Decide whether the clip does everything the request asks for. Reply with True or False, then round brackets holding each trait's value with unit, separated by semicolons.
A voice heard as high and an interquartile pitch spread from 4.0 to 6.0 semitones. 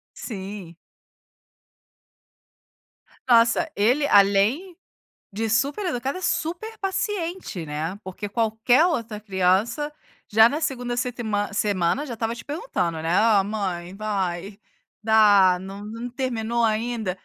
True (220 Hz; 4.3 semitones)